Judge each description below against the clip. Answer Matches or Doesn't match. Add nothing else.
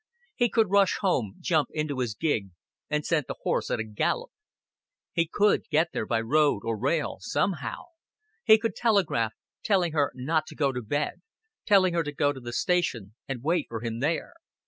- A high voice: Doesn't match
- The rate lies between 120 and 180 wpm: Doesn't match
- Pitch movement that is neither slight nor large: Doesn't match